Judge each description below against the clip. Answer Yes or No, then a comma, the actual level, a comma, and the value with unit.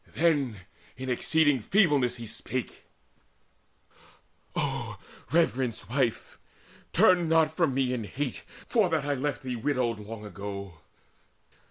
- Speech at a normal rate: No, slow, 120 wpm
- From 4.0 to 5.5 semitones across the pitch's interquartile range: Yes, average, 5.2 semitones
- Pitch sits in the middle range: No, low, 130 Hz